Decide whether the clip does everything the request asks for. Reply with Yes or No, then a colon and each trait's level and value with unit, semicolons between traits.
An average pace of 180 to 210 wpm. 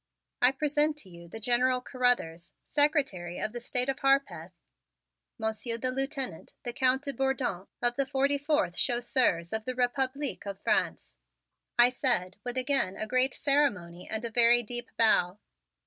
No: average, 160 wpm